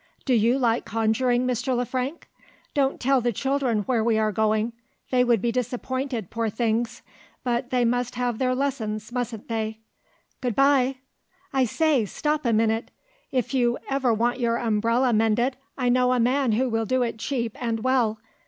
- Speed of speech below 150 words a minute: No, average, 175 wpm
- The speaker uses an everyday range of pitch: No, narrow, 2.3 semitones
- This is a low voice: No, high, 245 Hz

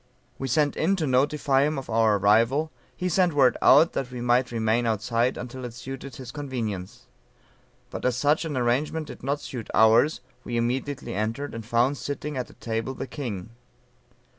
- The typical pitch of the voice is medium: No, low, 125 Hz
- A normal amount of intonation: Yes, average, 3.7 semitones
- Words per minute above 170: Yes, average, 180 wpm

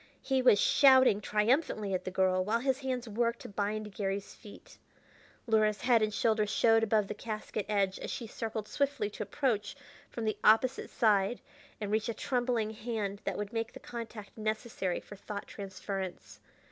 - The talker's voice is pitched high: Yes, high, 215 Hz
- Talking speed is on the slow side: No, average, 170 wpm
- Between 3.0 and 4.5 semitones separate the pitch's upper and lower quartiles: No, narrow, 2.5 semitones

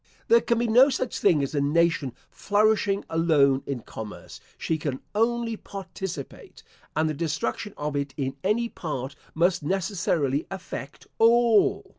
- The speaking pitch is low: No, medium, 170 Hz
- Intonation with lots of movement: Yes, wide, 6.9 semitones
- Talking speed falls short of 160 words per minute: Yes, average, 145 wpm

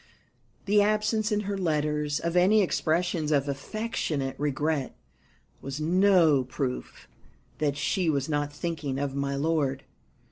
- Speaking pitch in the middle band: Yes, medium, 155 Hz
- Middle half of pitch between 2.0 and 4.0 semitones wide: No, average, 4.5 semitones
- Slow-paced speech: Yes, slow, 130 wpm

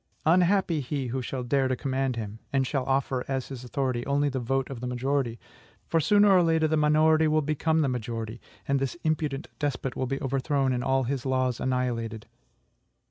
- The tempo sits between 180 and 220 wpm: Yes, average, 190 wpm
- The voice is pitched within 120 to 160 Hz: Yes, low, 135 Hz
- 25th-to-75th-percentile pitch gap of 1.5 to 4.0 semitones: Yes, average, 3.0 semitones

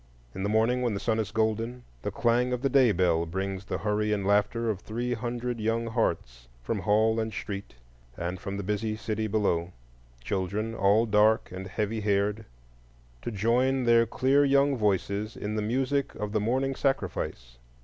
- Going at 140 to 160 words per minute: No, average, 170 wpm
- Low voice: Yes, low, 105 Hz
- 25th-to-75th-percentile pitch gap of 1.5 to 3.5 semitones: Yes, average, 3.2 semitones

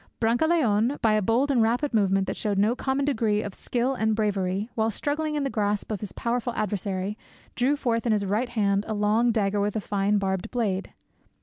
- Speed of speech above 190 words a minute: Yes, fast, 205 wpm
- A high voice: Yes, high, 220 Hz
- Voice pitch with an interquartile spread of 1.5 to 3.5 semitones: Yes, average, 3.1 semitones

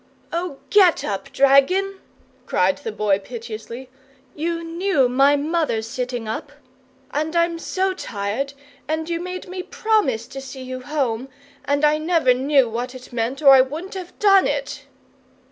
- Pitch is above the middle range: Yes, very high, 285 Hz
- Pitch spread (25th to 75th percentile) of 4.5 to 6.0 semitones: Yes, average, 5.3 semitones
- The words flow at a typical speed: Yes, average, 155 wpm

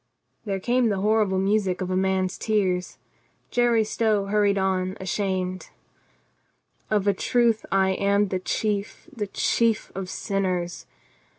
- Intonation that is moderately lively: No, narrow, 2.2 semitones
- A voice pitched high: Yes, high, 200 Hz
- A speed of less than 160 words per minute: Yes, slow, 135 wpm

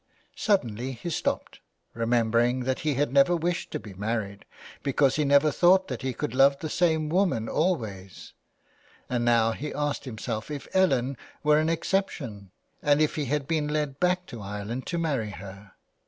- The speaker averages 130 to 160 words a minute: No, average, 170 wpm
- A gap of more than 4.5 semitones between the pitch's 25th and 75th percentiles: Yes, average, 5.2 semitones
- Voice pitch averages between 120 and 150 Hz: Yes, low, 135 Hz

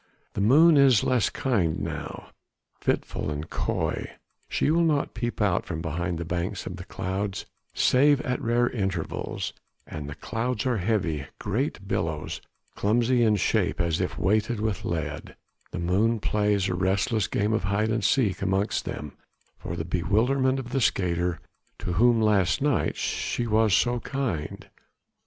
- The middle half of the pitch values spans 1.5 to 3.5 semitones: No, average, 5.2 semitones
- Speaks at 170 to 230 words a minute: No, average, 155 wpm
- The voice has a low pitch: Yes, low, 105 Hz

